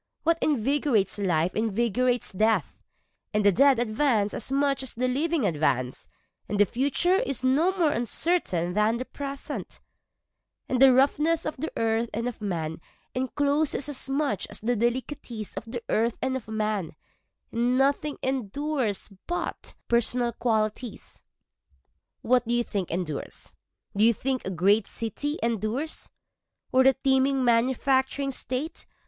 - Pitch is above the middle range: Yes, high, 245 Hz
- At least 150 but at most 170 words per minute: No, average, 140 wpm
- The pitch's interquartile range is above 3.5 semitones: Yes, average, 4.2 semitones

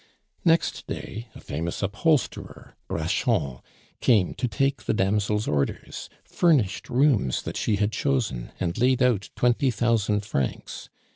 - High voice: No, low, 110 Hz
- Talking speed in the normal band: No, slow, 130 wpm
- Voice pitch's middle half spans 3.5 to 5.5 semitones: Yes, average, 4.5 semitones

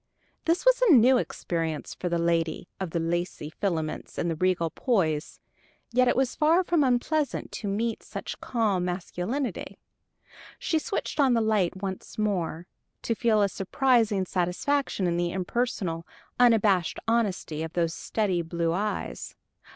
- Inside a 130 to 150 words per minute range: Yes, average, 145 wpm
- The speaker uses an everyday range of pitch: No, wide, 5.9 semitones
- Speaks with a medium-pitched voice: No, high, 195 Hz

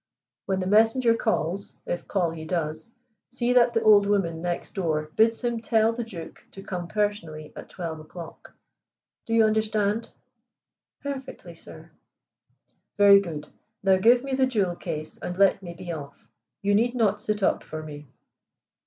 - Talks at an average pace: Yes, average, 160 wpm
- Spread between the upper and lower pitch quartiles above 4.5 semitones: Yes, average, 5.1 semitones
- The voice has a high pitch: Yes, high, 200 Hz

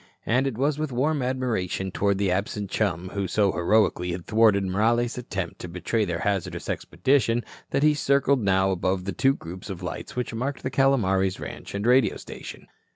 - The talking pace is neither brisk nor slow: Yes, average, 185 wpm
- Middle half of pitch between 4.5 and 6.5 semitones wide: Yes, average, 5.2 semitones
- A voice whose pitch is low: Yes, low, 105 Hz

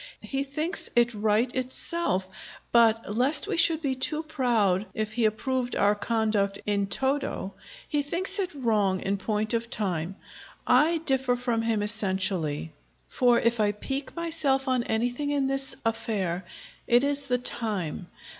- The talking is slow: No, average, 150 wpm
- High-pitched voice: Yes, high, 235 Hz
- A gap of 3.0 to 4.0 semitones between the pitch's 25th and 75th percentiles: No, average, 4.6 semitones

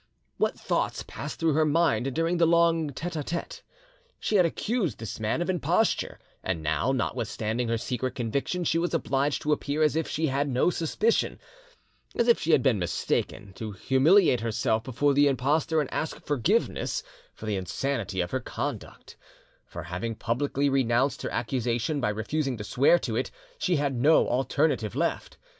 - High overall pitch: No, medium, 140 Hz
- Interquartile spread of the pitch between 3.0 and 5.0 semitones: No, wide, 5.6 semitones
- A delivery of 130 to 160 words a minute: No, average, 175 wpm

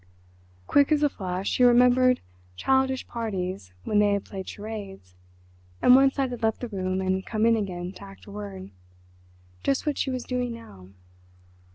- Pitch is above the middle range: Yes, high, 210 Hz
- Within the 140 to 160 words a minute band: No, average, 170 wpm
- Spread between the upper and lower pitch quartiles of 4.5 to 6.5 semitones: Yes, average, 5.1 semitones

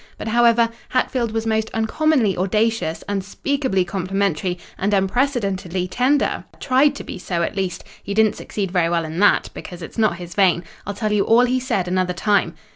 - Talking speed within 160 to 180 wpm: Yes, average, 170 wpm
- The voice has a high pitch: Yes, high, 205 Hz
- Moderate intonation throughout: Yes, average, 4.0 semitones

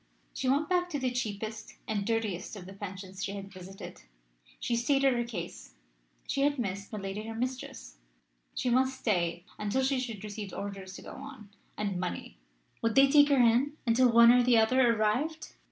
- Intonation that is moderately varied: Yes, average, 4.7 semitones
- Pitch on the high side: Yes, high, 225 Hz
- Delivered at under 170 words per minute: No, average, 185 wpm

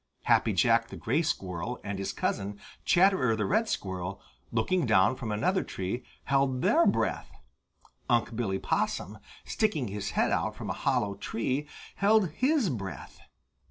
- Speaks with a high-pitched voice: No, low, 120 Hz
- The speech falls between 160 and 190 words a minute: No, average, 150 wpm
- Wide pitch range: Yes, wide, 8.4 semitones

